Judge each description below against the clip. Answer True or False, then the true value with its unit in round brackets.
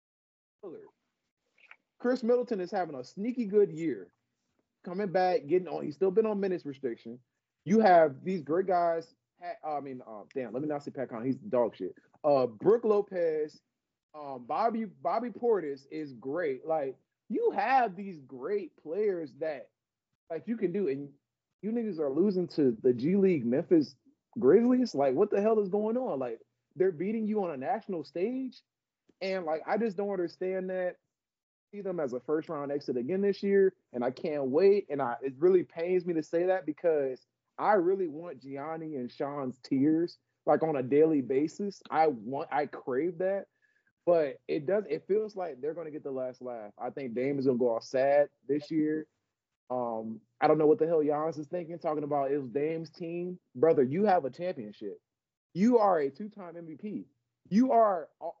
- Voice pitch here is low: False (180 Hz)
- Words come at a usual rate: True (185 wpm)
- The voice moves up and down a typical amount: False (7.4 semitones)